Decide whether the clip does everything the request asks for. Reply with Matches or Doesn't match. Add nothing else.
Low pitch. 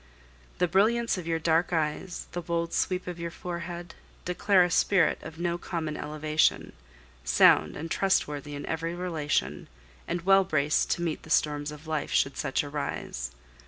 Doesn't match